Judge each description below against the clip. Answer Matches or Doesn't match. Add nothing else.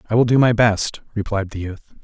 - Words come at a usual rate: Doesn't match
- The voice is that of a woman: Doesn't match